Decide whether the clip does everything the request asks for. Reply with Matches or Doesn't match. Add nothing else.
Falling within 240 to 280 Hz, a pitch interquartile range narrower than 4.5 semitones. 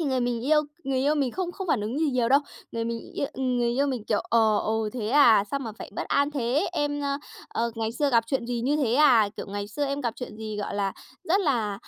Matches